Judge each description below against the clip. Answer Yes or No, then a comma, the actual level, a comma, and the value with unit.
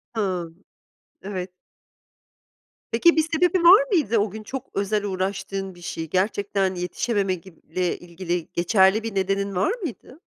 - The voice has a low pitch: No, high, 195 Hz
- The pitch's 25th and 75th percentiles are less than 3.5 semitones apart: Yes, average, 3.1 semitones